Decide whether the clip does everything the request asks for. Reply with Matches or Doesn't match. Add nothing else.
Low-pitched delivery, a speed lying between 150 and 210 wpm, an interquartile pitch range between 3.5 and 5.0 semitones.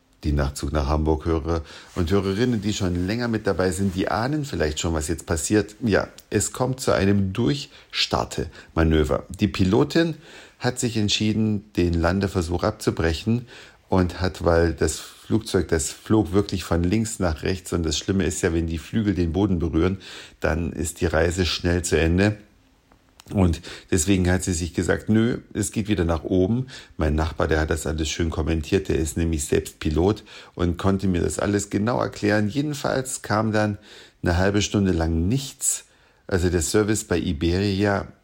Matches